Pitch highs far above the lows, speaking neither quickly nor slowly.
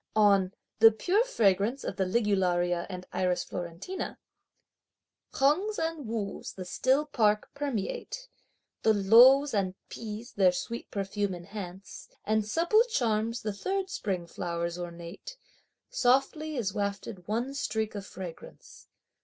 No: wide, 6.2 semitones; slow, 125 wpm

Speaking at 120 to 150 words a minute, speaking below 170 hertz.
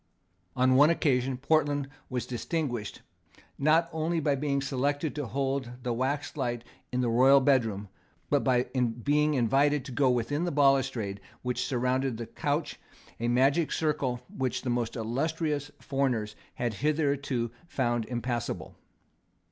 Yes: slow, 135 wpm; low, 135 Hz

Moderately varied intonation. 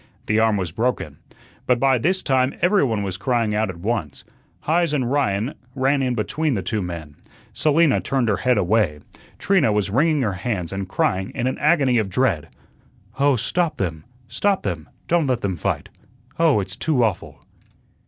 No: wide, 6.3 semitones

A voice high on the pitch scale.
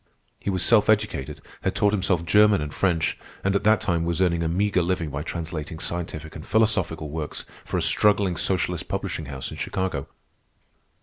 No: very low, 85 Hz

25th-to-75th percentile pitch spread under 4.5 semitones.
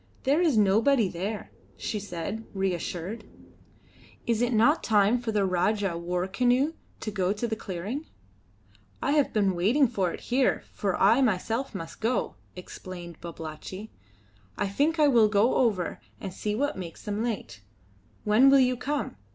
No: average, 4.8 semitones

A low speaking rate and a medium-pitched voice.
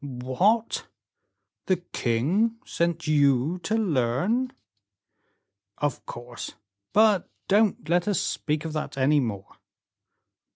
Yes: slow, 110 wpm; medium, 155 Hz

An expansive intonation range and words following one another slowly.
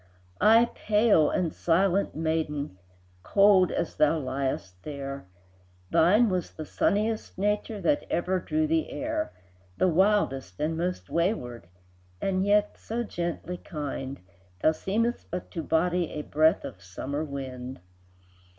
Yes: wide, 5.9 semitones; slow, 130 wpm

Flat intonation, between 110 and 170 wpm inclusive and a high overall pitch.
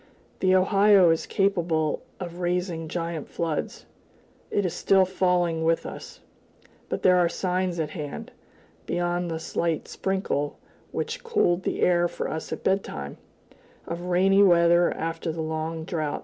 No: narrow, 2.3 semitones; average, 145 wpm; medium, 175 Hz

